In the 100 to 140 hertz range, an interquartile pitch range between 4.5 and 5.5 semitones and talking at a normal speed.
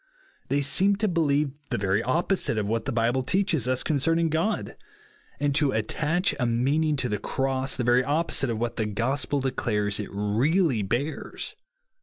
Yes: low, 135 Hz; average, 5.2 semitones; average, 170 wpm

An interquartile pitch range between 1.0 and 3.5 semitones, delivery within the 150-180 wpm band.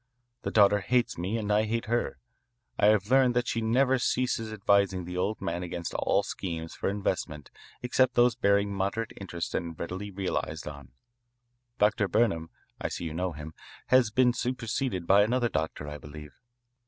No: average, 5.3 semitones; average, 170 wpm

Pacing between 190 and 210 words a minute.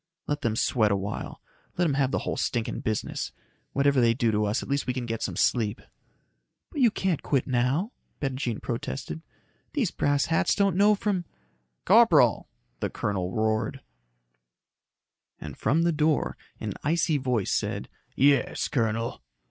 No: average, 160 wpm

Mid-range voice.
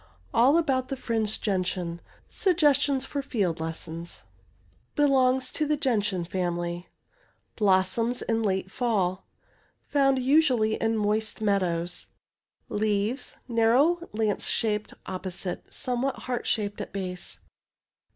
No: high, 220 Hz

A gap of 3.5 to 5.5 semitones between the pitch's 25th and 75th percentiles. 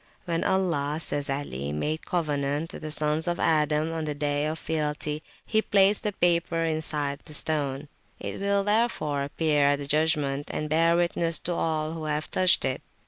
No: narrow, 2.4 semitones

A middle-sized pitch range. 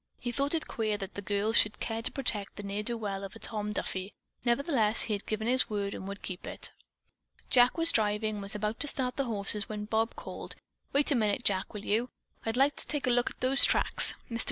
Yes: average, 3.1 semitones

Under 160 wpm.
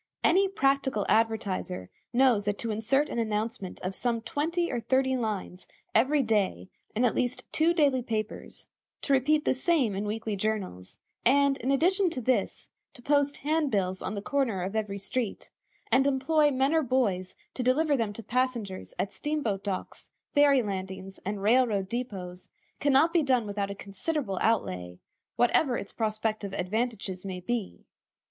No: average, 165 wpm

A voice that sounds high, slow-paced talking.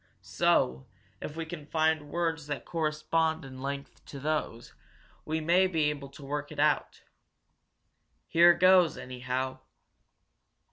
No: medium, 150 Hz; slow, 130 wpm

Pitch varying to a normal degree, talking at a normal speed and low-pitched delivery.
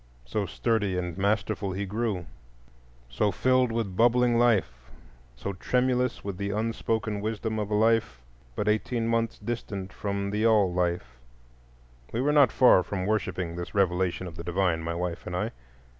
Yes: average, 4.3 semitones; average, 160 wpm; low, 100 Hz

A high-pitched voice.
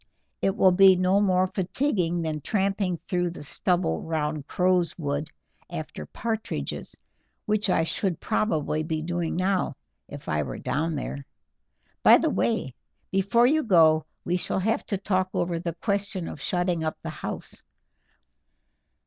No: medium, 180 Hz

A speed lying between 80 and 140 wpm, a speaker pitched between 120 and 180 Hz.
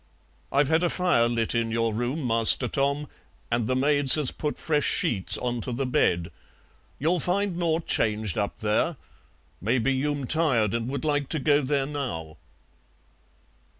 No: average, 160 wpm; low, 135 Hz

